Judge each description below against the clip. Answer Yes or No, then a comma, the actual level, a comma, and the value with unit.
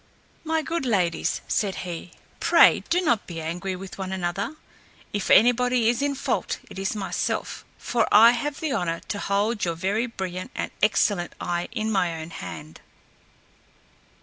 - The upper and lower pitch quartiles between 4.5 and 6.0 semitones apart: Yes, average, 5.2 semitones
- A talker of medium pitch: No, high, 200 Hz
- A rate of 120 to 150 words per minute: No, average, 160 wpm